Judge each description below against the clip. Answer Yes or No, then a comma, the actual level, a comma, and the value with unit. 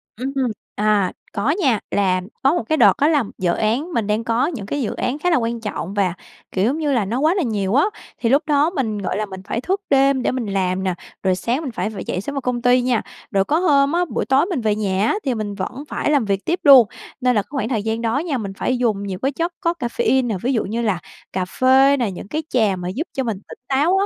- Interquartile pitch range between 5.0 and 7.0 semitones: Yes, wide, 5.4 semitones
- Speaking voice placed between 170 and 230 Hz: No, high, 240 Hz